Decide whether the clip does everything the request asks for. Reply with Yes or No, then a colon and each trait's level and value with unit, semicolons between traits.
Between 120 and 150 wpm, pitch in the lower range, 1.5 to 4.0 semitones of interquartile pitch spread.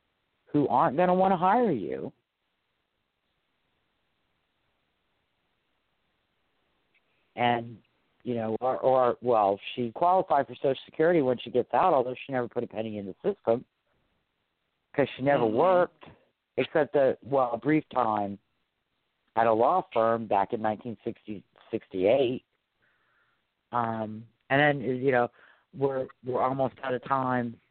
Yes: slow, 135 wpm; low, 125 Hz; average, 3.3 semitones